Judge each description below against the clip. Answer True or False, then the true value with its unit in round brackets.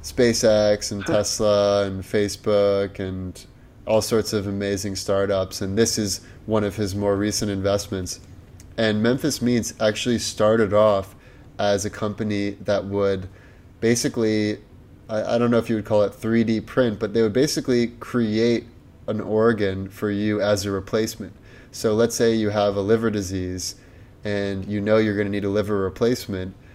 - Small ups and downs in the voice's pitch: True (2.1 semitones)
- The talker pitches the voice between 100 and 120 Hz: True (105 Hz)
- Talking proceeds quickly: False (160 wpm)